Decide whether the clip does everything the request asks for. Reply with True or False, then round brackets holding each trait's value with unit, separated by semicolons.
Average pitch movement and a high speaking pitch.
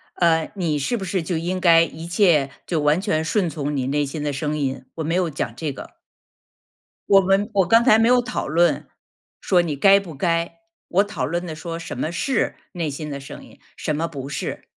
False (3.9 semitones; 165 Hz)